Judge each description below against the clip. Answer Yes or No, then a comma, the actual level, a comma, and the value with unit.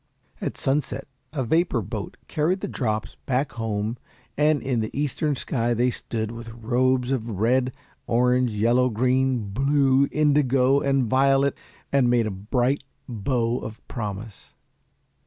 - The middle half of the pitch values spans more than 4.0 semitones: No, average, 3.1 semitones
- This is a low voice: Yes, low, 125 Hz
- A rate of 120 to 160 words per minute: Yes, average, 140 wpm